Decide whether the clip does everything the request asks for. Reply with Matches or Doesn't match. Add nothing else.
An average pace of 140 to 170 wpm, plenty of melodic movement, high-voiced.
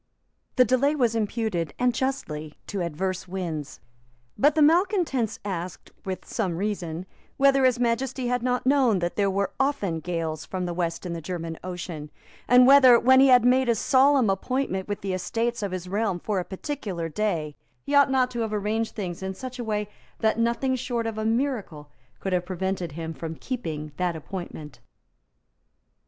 Doesn't match